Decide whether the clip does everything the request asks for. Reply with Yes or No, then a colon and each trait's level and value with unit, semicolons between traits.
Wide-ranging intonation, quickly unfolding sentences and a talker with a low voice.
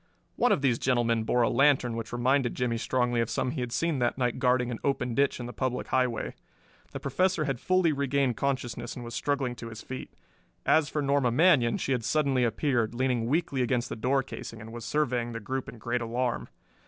No: average, 2.7 semitones; fast, 215 wpm; low, 125 Hz